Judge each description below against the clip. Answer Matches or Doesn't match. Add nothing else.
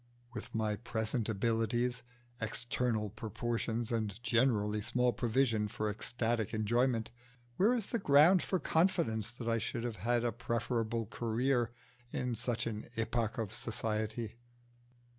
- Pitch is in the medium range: Doesn't match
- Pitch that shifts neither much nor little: Doesn't match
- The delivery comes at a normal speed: Doesn't match